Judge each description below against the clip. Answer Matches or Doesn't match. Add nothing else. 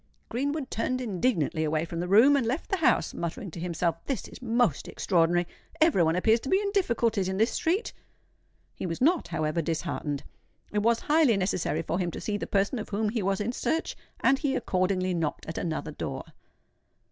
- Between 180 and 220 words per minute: Matches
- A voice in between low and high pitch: Doesn't match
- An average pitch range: Doesn't match